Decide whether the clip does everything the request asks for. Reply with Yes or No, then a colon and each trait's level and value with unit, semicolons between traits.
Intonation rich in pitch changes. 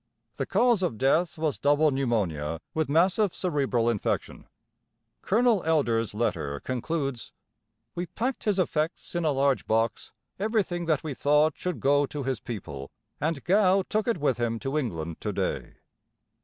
Yes: wide, 6.9 semitones